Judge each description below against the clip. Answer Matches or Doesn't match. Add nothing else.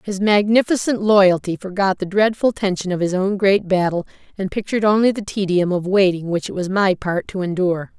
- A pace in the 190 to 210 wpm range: Matches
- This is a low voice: Doesn't match